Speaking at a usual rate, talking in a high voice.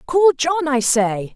Yes: average, 175 wpm; very high, 280 Hz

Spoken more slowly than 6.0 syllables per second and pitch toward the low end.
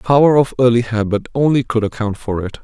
No: 6.2 syllables/s; low, 120 Hz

